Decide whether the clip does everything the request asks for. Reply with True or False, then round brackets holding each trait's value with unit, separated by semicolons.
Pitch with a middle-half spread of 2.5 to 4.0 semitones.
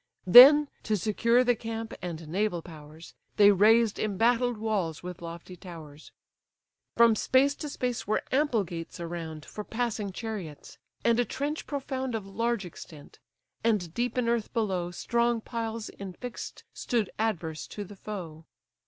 False (5.1 semitones)